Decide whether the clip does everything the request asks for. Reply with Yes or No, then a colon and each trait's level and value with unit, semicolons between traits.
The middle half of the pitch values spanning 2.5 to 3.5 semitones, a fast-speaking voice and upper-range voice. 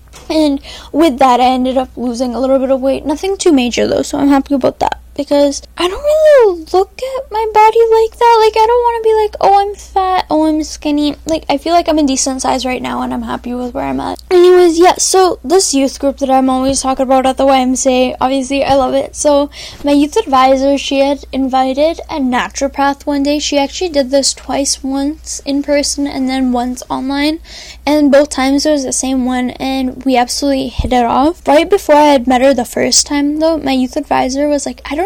Yes: average, 3.1 semitones; fast, 230 wpm; very high, 280 Hz